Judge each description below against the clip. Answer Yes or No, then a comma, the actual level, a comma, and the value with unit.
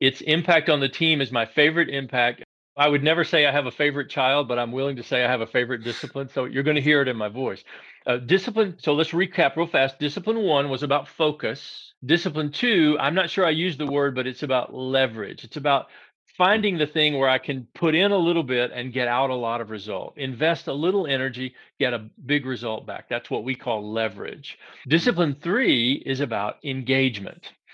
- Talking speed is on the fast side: Yes, fast, 220 wpm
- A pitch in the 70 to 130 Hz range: No, medium, 140 Hz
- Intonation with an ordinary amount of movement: Yes, average, 3.6 semitones